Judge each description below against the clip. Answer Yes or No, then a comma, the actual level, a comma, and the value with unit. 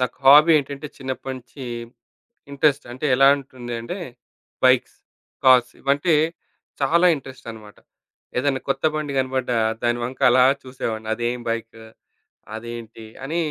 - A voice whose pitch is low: Yes, low, 130 Hz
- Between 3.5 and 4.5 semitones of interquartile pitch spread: No, average, 2.7 semitones